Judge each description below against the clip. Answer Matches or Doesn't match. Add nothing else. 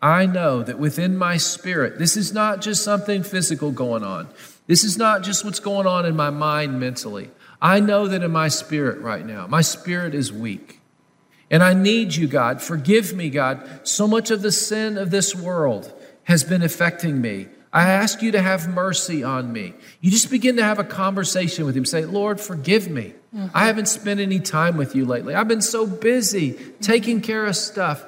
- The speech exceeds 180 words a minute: Matches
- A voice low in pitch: Doesn't match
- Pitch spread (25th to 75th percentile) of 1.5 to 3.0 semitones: Doesn't match